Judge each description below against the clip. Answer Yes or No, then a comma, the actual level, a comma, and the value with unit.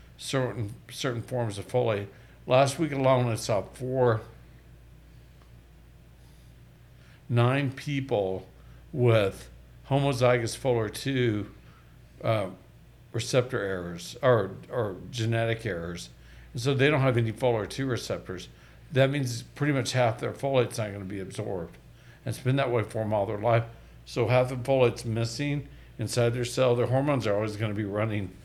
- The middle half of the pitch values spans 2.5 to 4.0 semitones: Yes, average, 3.7 semitones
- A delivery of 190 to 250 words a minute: No, average, 150 wpm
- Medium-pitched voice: No, low, 120 Hz